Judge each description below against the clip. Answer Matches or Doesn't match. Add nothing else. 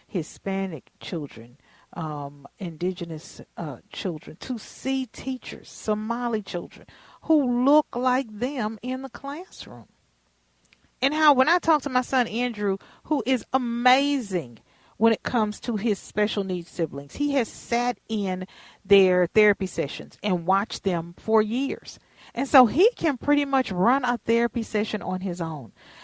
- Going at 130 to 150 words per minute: Matches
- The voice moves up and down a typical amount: Doesn't match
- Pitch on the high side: Matches